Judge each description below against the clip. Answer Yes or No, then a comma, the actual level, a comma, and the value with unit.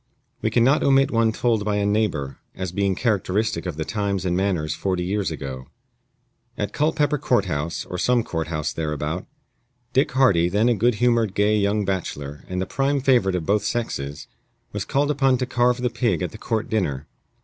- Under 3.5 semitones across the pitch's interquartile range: No, wide, 5.6 semitones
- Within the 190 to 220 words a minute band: Yes, average, 195 wpm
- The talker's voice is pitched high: No, low, 100 Hz